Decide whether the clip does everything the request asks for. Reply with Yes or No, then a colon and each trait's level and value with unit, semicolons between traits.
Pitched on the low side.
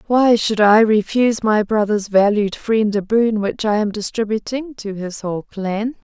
No: high, 215 Hz